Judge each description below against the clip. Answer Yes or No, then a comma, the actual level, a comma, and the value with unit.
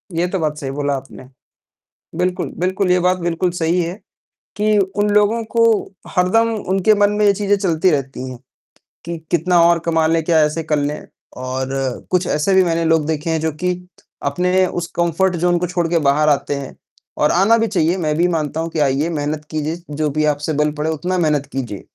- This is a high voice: No, medium, 165 Hz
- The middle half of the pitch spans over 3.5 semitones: No, average, 3.2 semitones